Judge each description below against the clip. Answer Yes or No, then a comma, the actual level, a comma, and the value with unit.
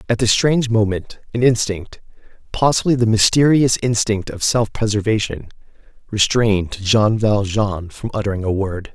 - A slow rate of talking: Yes, slow, 120 wpm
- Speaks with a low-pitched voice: Yes, low, 110 Hz